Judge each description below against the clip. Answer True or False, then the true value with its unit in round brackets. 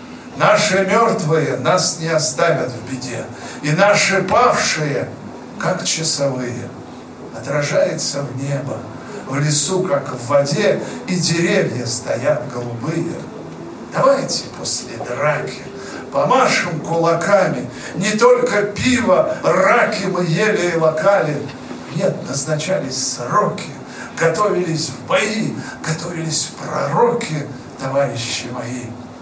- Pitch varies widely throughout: True (6.1 semitones)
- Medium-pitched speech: True (155 Hz)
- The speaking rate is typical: False (100 wpm)